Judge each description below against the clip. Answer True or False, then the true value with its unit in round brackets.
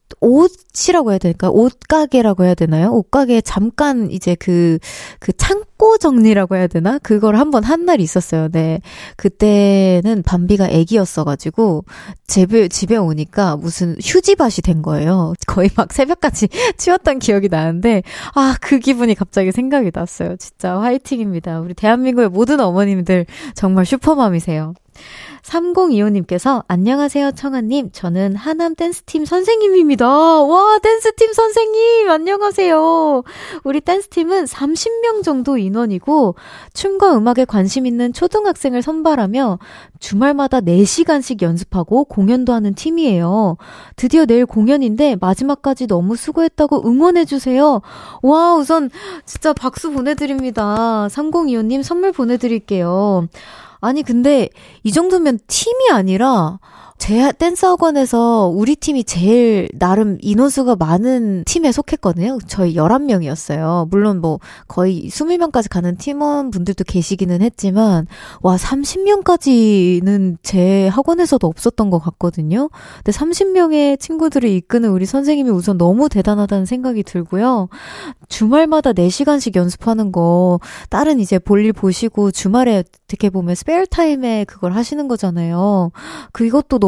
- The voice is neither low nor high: False (235 Hz)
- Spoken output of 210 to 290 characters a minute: False (305 characters per minute)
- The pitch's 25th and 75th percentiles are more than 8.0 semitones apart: False (7.7 semitones)